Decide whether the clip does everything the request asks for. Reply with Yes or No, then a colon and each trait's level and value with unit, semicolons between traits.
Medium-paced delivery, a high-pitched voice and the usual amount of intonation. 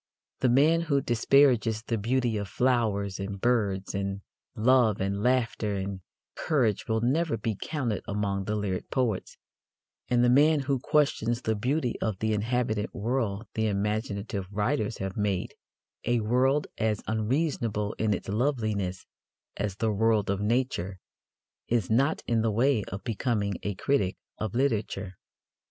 No: average, 145 wpm; low, 110 Hz; average, 3.7 semitones